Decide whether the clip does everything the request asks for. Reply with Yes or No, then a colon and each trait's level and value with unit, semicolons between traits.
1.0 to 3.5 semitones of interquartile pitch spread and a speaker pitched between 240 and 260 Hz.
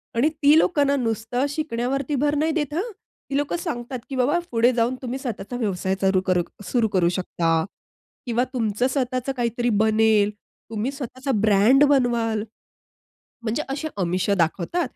No: average, 4.3 semitones; high, 245 Hz